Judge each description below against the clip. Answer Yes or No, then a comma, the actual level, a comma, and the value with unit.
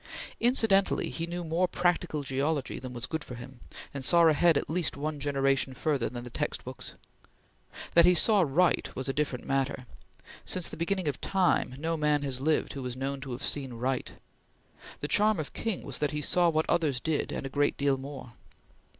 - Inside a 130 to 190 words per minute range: No, average, 200 wpm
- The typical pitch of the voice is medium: Yes, medium, 145 Hz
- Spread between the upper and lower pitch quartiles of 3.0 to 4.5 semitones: Yes, average, 4.0 semitones